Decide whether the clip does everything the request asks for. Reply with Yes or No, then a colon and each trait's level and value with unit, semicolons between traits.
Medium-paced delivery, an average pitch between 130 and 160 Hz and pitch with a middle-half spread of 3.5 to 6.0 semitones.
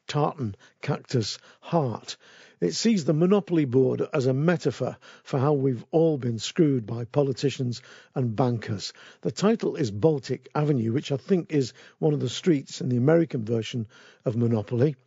Yes: average, 160 wpm; medium, 140 Hz; average, 4.1 semitones